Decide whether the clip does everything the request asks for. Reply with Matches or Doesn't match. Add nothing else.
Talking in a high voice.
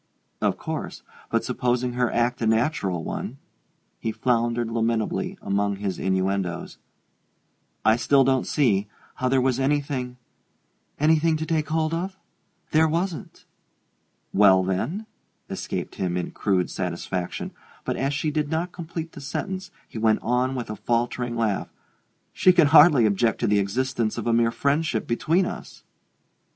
Doesn't match